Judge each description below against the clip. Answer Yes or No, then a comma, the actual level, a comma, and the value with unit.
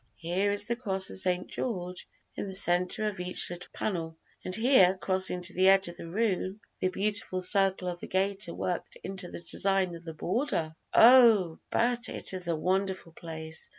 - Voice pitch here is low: No, medium, 185 Hz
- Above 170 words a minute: Yes, average, 185 wpm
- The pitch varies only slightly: Yes, narrow, 2.3 semitones